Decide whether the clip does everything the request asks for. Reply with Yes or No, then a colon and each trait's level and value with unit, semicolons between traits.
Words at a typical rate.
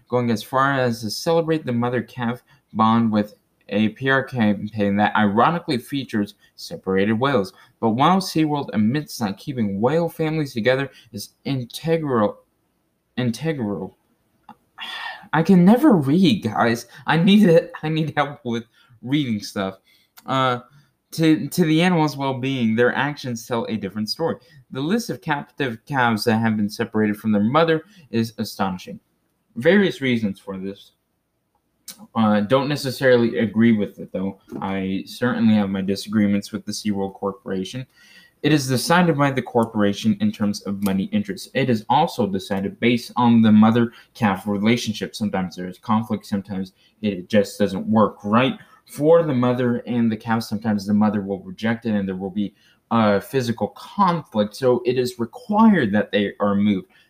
Yes: average, 155 wpm